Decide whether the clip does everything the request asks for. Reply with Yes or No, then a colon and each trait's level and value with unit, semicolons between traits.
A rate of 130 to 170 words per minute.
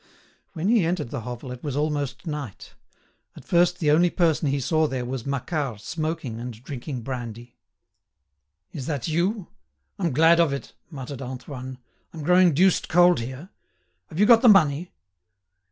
Yes: average, 160 wpm